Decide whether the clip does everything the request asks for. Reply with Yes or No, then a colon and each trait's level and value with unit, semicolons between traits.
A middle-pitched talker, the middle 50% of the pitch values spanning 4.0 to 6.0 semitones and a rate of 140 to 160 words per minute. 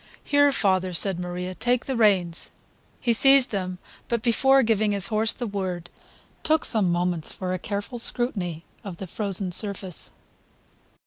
No: high, 200 Hz; average, 4.5 semitones; average, 150 wpm